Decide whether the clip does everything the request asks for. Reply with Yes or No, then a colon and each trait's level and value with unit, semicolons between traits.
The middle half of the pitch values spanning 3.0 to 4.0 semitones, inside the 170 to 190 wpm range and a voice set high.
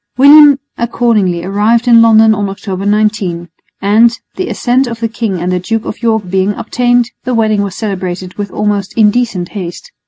Yes: average, 3.3 semitones; average, 175 wpm; high, 215 Hz